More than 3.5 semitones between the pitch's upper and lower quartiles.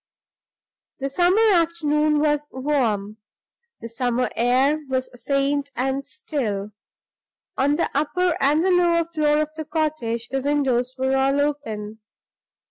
No: average, 3.2 semitones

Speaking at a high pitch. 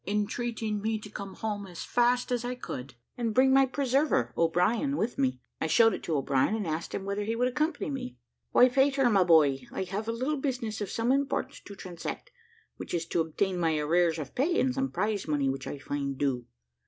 Yes: high, 210 Hz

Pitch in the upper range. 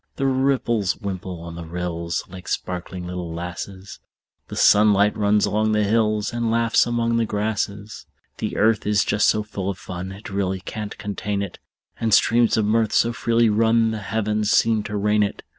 No: low, 105 Hz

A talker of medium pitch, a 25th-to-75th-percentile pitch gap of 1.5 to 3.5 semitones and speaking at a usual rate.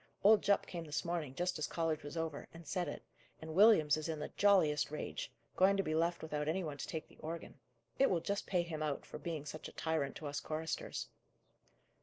No: medium, 160 Hz; narrow, 2.6 semitones; fast, 225 wpm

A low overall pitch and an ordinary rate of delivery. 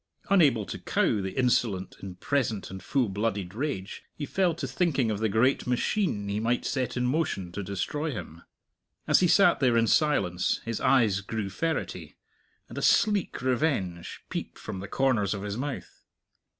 Yes: low, 115 Hz; average, 175 wpm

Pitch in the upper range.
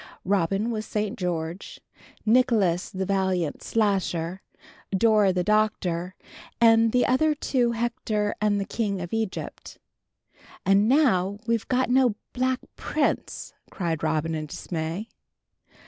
Yes: high, 205 Hz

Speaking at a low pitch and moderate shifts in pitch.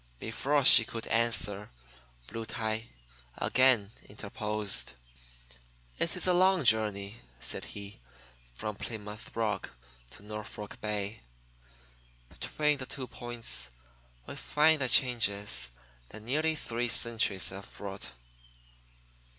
Yes: low, 110 Hz; average, 3.7 semitones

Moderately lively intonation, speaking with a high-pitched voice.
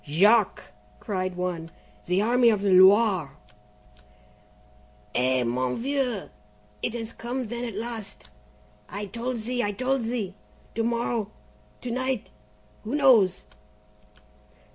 Yes: average, 4.4 semitones; high, 220 Hz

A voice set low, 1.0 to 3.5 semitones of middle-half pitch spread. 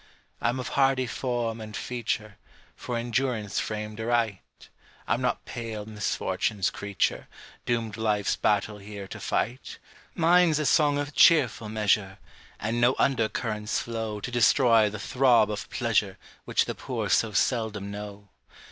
Yes: low, 110 Hz; average, 2.7 semitones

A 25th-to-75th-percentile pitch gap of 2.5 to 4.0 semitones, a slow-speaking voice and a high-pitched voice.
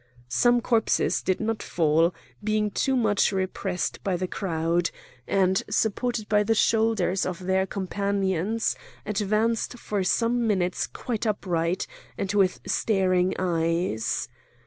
Yes: average, 3.2 semitones; slow, 125 wpm; high, 195 Hz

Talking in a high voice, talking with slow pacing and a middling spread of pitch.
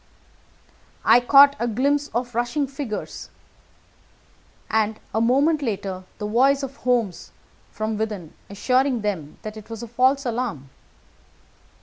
Yes: high, 235 Hz; slow, 125 wpm; average, 4.1 semitones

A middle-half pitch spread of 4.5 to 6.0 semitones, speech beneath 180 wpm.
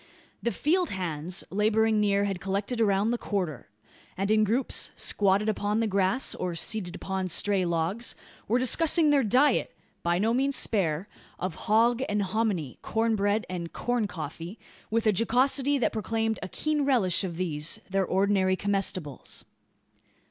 No: average, 3.7 semitones; average, 155 wpm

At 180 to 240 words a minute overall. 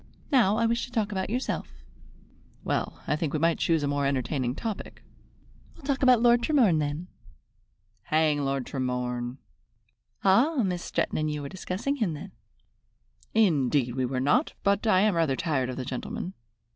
No: average, 170 wpm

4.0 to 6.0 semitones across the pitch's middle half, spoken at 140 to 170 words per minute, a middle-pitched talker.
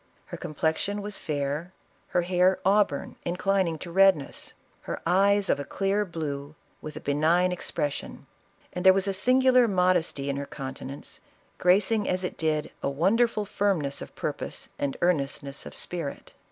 Yes: average, 4.8 semitones; average, 165 wpm; medium, 180 Hz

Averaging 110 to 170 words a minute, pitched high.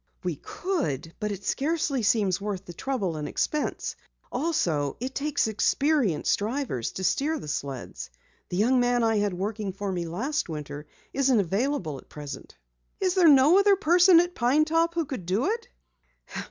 Yes: average, 165 wpm; high, 230 Hz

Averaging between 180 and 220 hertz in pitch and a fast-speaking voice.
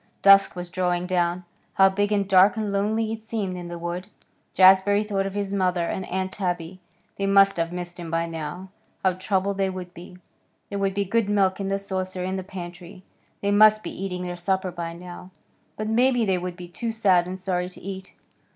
Yes: high, 190 Hz; fast, 210 wpm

